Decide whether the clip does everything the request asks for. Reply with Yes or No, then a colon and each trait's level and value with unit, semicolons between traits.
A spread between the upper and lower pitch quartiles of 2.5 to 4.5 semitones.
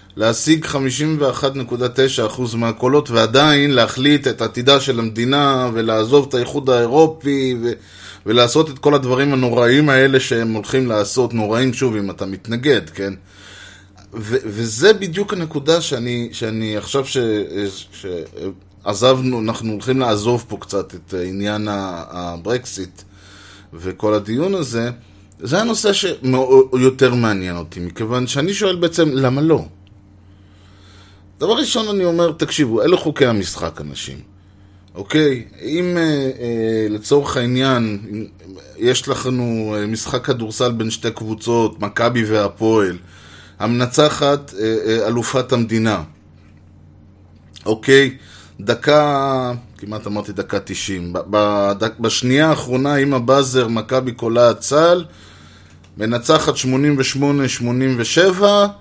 No: average, 5.1 semitones